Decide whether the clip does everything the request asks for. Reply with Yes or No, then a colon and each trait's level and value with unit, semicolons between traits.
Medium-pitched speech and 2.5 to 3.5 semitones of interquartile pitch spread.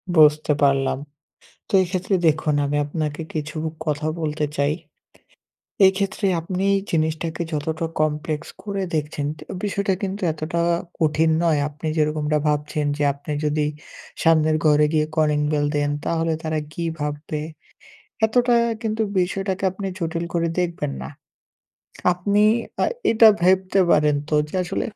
Yes: medium, 155 Hz; average, 3.2 semitones